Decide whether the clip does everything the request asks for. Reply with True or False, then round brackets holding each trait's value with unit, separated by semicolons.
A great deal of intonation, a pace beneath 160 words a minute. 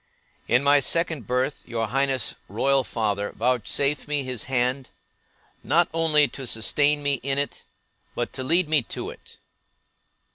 False (2.9 semitones; 145 wpm)